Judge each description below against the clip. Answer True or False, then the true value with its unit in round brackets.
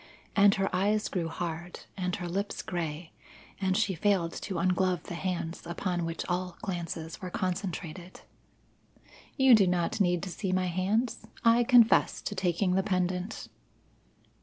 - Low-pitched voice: False (185 Hz)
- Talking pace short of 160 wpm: True (150 wpm)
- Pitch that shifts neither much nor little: False (2.2 semitones)